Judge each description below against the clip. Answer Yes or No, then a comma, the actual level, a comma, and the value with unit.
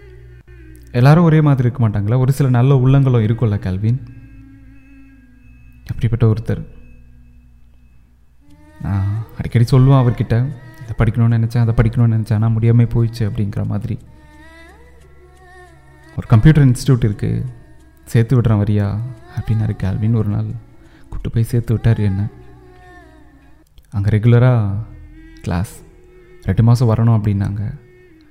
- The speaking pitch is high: No, low, 110 Hz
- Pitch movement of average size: No, wide, 7.1 semitones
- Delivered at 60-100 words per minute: No, average, 110 wpm